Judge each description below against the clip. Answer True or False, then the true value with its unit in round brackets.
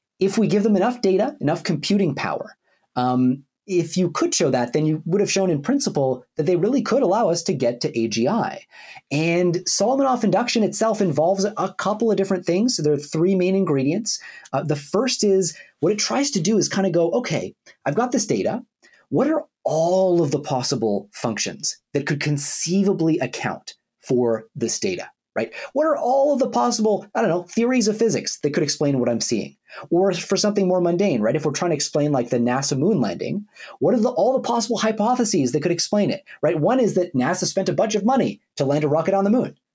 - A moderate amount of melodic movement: False (6.1 semitones)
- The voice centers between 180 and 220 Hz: True (190 Hz)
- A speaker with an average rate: False (215 wpm)